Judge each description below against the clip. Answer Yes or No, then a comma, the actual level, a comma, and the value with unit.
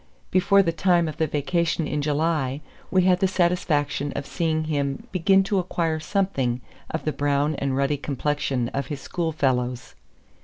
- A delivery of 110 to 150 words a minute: No, average, 160 wpm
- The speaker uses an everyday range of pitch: Yes, average, 3.8 semitones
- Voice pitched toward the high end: No, medium, 155 Hz